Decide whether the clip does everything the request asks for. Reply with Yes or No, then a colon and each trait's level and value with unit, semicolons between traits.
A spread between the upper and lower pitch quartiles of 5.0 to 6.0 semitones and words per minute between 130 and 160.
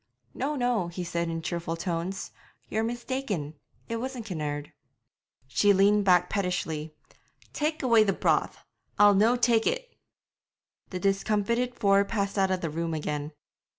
Yes: average, 5.3 semitones; average, 145 wpm